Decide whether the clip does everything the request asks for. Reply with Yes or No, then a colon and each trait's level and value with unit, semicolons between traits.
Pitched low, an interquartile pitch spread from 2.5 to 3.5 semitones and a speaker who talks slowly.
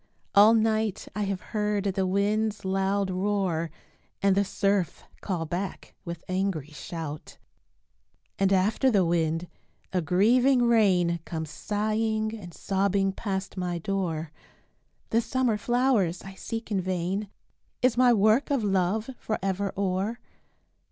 No: high, 195 Hz; average, 3.0 semitones; slow, 130 wpm